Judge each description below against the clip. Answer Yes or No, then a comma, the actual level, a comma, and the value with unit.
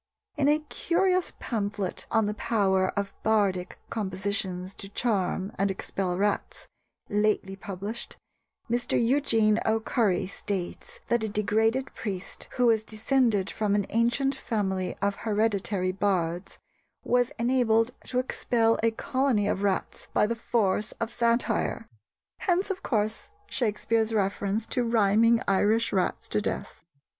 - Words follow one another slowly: Yes, slow, 130 wpm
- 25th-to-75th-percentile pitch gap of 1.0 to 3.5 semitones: Yes, average, 2.9 semitones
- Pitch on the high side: Yes, high, 215 Hz